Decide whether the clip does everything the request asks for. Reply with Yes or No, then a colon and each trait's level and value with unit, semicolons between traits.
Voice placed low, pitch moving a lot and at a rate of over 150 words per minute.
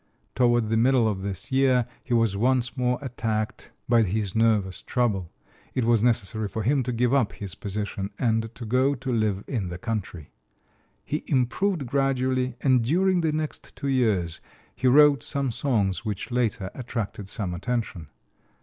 No: low, 120 Hz; average, 3.7 semitones; average, 165 wpm